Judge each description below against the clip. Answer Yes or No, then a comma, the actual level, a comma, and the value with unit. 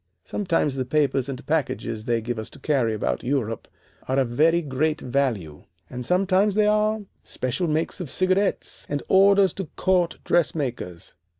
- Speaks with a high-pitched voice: No, medium, 145 Hz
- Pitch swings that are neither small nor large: No, wide, 6.8 semitones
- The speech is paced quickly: No, average, 160 wpm